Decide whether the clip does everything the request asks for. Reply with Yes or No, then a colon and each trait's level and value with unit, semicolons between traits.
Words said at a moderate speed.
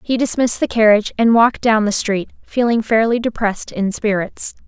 Yes: average, 180 wpm